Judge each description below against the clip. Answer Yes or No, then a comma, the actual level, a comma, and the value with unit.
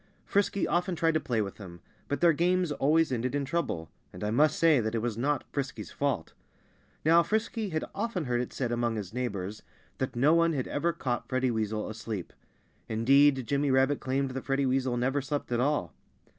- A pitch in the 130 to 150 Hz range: Yes, low, 135 Hz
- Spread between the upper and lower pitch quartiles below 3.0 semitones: No, average, 4.7 semitones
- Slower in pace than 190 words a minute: No, average, 200 wpm